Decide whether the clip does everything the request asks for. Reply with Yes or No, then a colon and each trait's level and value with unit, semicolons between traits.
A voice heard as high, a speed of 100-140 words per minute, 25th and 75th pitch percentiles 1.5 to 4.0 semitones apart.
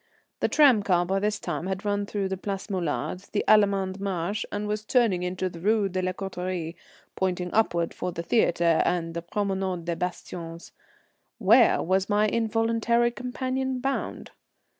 No: high, 195 Hz; average, 160 wpm; average, 3.2 semitones